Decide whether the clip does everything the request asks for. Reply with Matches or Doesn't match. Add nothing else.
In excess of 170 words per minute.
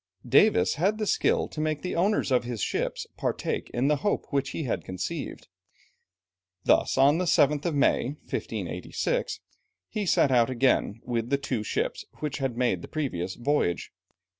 Doesn't match